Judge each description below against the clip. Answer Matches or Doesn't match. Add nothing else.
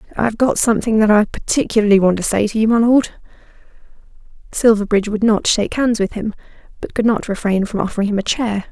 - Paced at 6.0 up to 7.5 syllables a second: Matches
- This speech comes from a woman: Matches